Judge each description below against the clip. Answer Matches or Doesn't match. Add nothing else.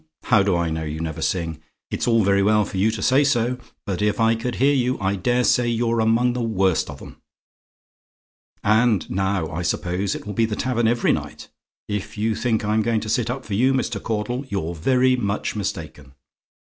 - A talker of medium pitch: Doesn't match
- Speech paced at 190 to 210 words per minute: Matches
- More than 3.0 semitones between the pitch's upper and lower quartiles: Matches